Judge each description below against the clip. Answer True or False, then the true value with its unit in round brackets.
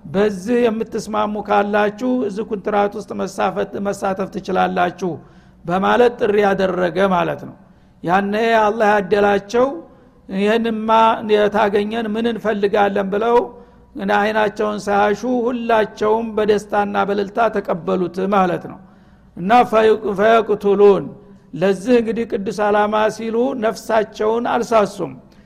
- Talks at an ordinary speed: True (90 wpm)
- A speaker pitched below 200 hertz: False (210 Hz)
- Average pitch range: False (2.0 semitones)